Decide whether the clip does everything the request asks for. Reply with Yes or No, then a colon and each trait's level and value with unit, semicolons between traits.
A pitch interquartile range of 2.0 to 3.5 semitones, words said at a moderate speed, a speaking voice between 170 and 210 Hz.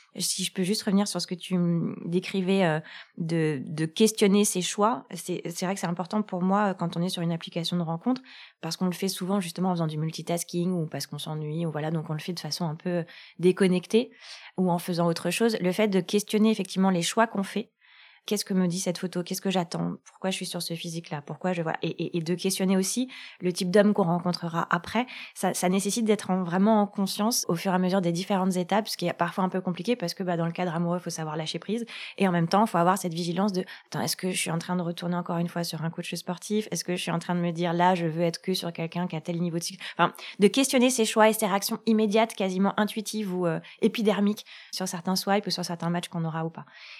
No: average, 2.8 semitones; fast, 270 wpm; medium, 185 Hz